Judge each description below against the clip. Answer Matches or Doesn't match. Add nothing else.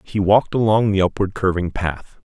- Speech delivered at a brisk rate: Doesn't match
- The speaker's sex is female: Doesn't match